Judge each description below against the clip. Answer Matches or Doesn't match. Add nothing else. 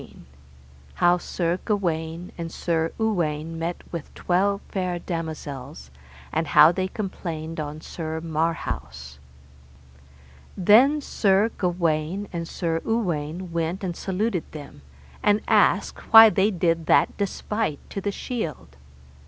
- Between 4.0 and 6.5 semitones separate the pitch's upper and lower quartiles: Doesn't match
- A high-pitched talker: Doesn't match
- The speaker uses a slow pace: Matches